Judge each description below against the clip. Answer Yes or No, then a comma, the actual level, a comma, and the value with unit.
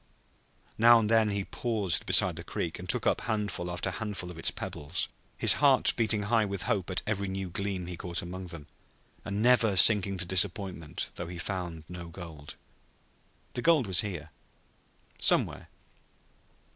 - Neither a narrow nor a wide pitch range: Yes, average, 3.2 semitones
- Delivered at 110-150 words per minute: No, average, 165 wpm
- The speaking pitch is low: Yes, very low, 95 Hz